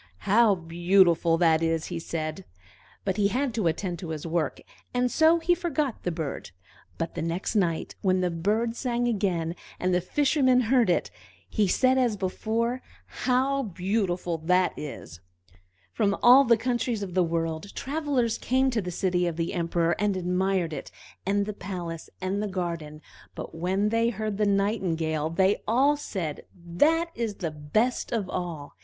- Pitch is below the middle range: No, high, 190 Hz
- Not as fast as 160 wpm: No, average, 170 wpm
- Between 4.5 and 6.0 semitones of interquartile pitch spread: Yes, wide, 5.6 semitones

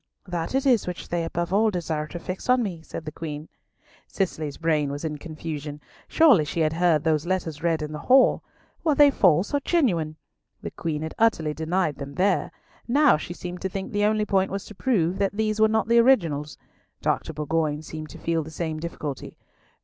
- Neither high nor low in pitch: Yes, medium, 170 Hz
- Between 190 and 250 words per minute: Yes, fast, 205 wpm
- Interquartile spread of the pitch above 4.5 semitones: Yes, average, 5.0 semitones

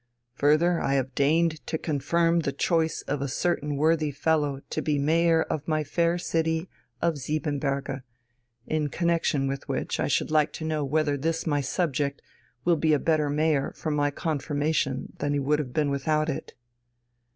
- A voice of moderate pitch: Yes, medium, 150 Hz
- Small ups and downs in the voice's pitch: Yes, narrow, 2.3 semitones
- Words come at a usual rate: Yes, average, 175 wpm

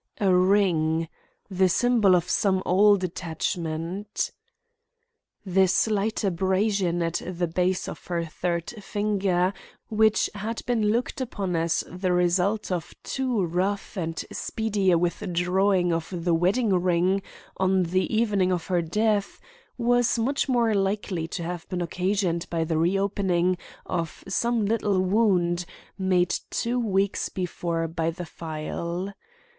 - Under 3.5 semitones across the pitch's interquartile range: Yes, average, 3.0 semitones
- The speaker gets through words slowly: Yes, slow, 130 wpm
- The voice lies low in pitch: No, medium, 185 Hz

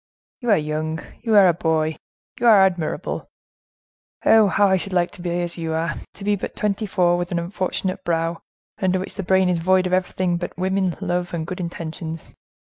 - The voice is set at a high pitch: No, medium, 180 Hz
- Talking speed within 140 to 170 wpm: No, average, 200 wpm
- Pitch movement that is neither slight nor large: No, narrow, 2.2 semitones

